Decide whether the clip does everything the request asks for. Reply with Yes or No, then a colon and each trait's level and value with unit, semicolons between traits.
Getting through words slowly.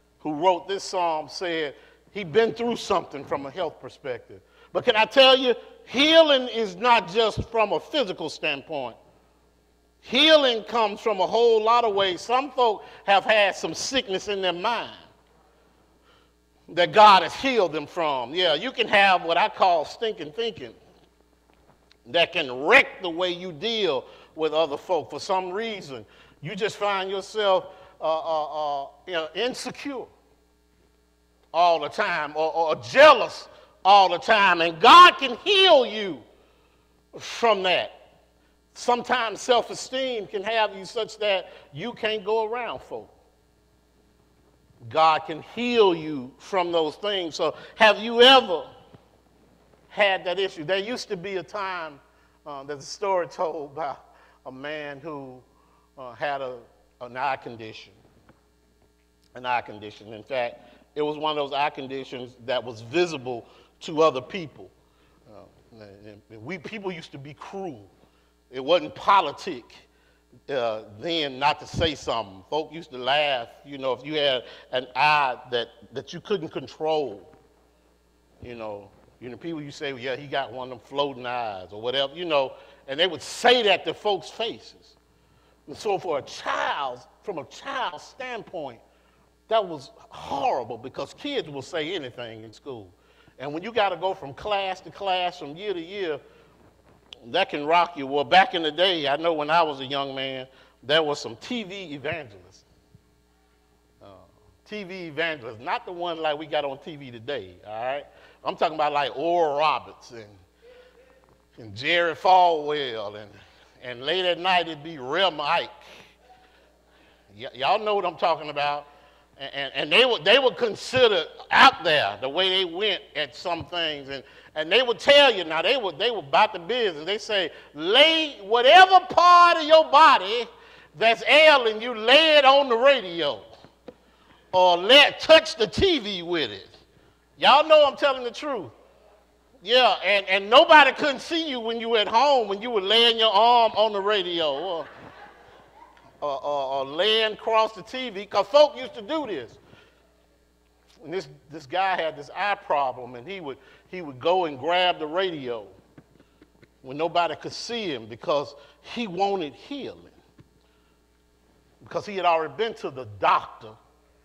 No: average, 165 wpm